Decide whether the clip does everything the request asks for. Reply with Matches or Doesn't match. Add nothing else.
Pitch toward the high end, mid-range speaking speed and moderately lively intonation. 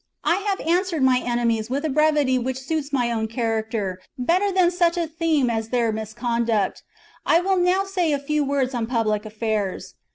Doesn't match